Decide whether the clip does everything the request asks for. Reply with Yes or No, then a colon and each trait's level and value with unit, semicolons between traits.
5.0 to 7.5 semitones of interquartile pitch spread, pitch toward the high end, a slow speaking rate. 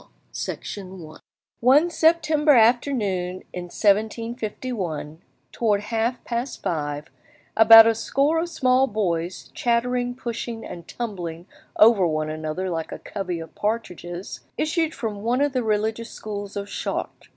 Yes: average, 5.3 semitones; high, 220 Hz; slow, 130 wpm